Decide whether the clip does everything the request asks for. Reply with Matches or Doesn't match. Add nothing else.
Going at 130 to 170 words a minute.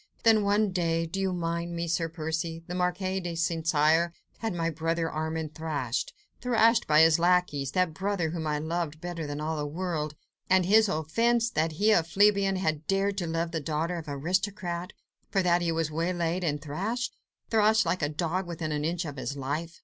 Doesn't match